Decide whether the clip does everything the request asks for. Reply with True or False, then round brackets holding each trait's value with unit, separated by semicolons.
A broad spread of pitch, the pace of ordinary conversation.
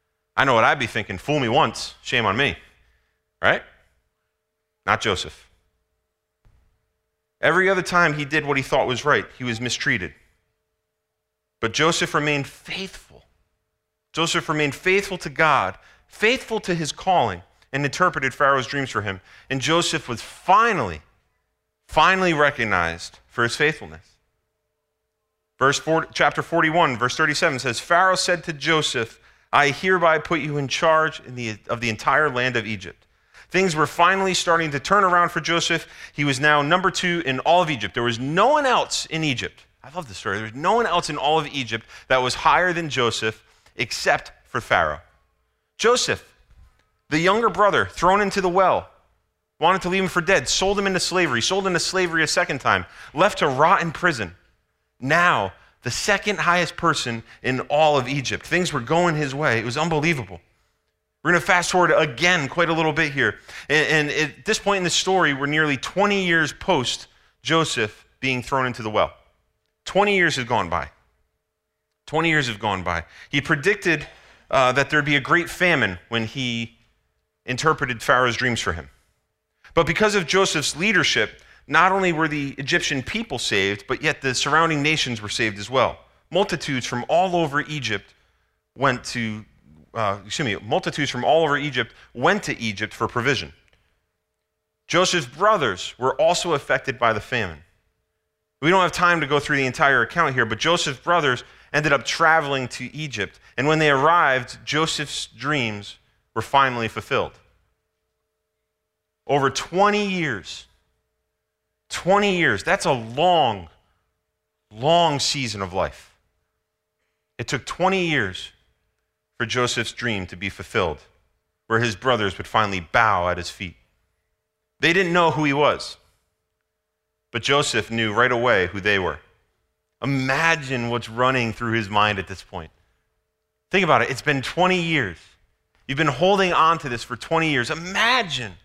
True (8.8 semitones; 165 wpm)